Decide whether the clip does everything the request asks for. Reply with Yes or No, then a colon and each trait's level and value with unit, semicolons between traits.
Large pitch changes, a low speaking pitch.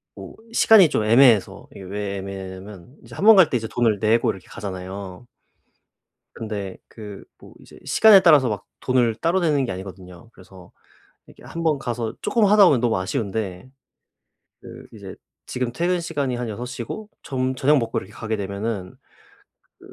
Yes: wide, 6.1 semitones; low, 115 Hz